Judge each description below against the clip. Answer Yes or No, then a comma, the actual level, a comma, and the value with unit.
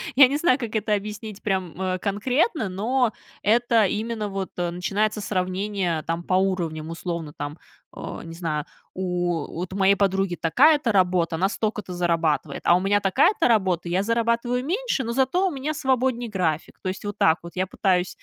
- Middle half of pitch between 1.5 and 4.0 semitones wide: No, average, 4.7 semitones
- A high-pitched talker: Yes, high, 195 Hz